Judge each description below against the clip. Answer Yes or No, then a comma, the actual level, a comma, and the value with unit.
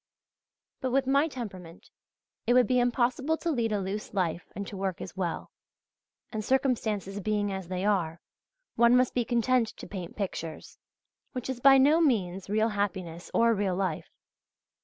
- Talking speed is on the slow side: No, average, 165 wpm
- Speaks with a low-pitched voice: No, high, 210 Hz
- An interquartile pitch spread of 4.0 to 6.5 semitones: Yes, average, 4.8 semitones